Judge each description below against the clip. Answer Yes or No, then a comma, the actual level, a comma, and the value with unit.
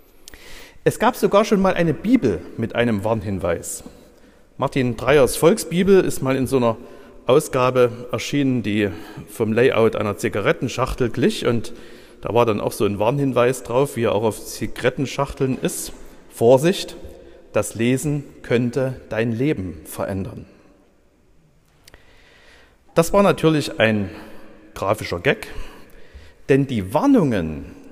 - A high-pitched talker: No, low, 130 Hz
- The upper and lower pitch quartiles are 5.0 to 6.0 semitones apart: Yes, wide, 5.5 semitones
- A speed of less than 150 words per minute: Yes, slow, 125 wpm